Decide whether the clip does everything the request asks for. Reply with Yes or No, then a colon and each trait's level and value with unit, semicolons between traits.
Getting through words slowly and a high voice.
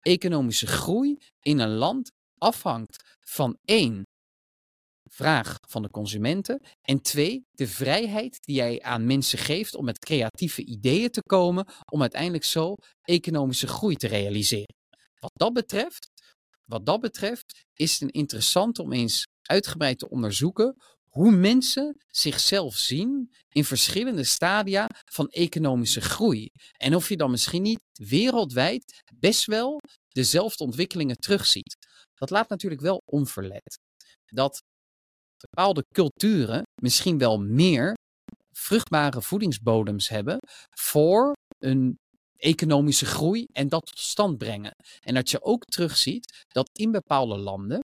No: slow, 130 wpm; medium, 155 Hz